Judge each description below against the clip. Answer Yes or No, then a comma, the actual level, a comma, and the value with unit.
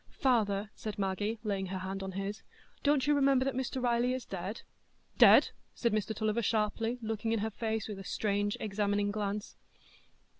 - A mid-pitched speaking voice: No, high, 215 Hz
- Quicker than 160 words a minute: Yes, average, 175 wpm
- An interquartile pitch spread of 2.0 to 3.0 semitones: Yes, average, 2.7 semitones